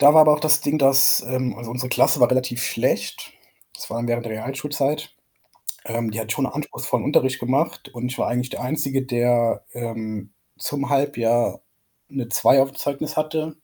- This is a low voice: Yes, low, 130 Hz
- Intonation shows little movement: No, average, 3.2 semitones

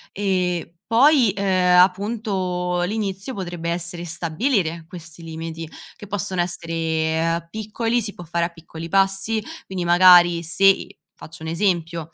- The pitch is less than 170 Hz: No, medium, 180 Hz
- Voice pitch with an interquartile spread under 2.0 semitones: No, average, 2.7 semitones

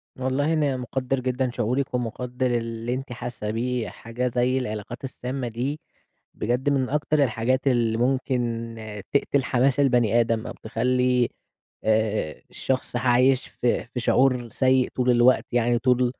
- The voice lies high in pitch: No, low, 125 Hz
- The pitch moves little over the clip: Yes, narrow, 1.7 semitones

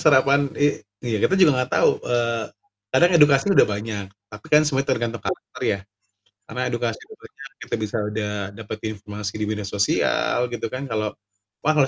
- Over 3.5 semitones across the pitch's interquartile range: Yes, average, 4.5 semitones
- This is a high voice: No, low, 115 Hz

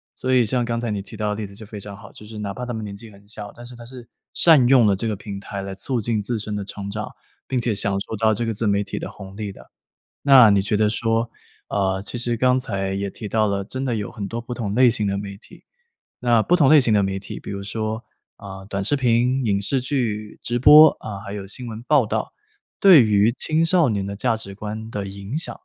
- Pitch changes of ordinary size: Yes, average, 3.3 semitones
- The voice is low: Yes, low, 110 Hz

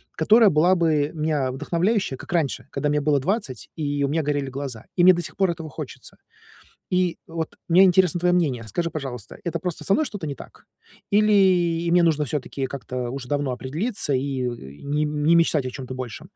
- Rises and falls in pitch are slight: No, average, 4.3 semitones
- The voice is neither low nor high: Yes, medium, 155 Hz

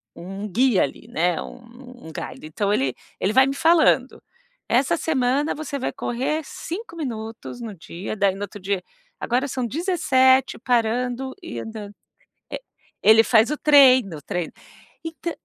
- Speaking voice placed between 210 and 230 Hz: No, high, 245 Hz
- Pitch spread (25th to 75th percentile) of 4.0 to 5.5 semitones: Yes, average, 5.0 semitones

